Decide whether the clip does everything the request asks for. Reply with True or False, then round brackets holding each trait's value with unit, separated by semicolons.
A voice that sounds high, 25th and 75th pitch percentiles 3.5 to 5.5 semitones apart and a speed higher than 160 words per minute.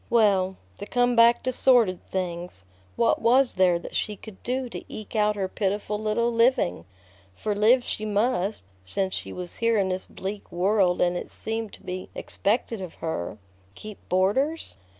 True (210 Hz; 3.9 semitones; 170 wpm)